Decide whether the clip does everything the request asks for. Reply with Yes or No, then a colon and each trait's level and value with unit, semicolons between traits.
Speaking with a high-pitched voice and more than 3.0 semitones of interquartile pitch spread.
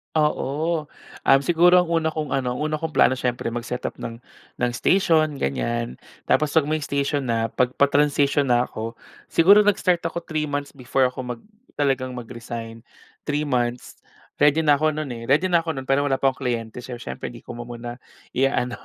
No: low, 135 Hz; average, 4.0 semitones